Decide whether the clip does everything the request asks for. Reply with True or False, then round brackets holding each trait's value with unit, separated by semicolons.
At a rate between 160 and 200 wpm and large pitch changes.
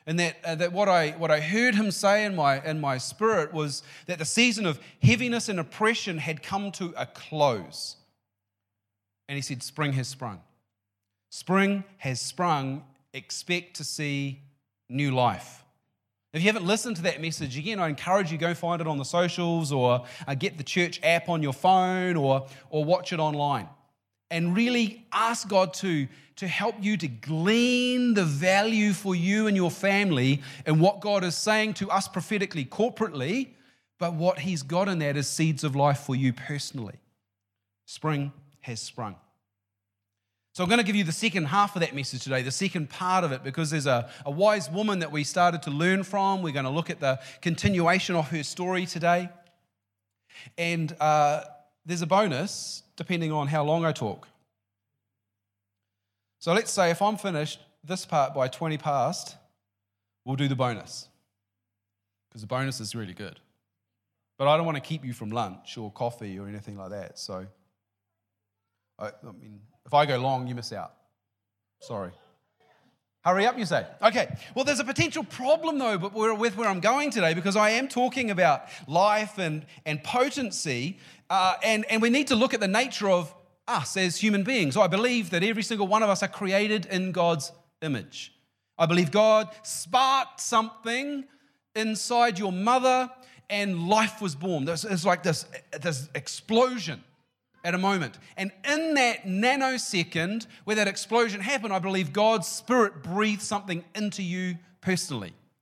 True (175 wpm; 7.0 semitones)